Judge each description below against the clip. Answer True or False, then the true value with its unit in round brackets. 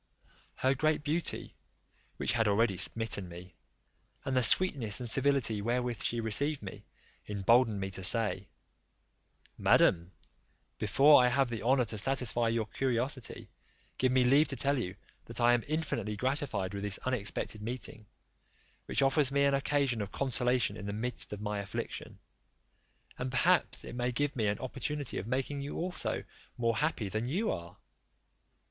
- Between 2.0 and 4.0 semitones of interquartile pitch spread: False (4.5 semitones)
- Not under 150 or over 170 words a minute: True (160 wpm)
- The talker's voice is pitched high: False (120 Hz)